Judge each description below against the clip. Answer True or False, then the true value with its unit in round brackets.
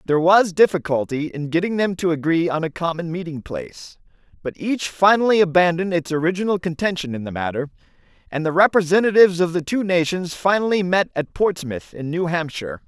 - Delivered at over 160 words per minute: True (170 wpm)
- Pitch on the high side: False (170 Hz)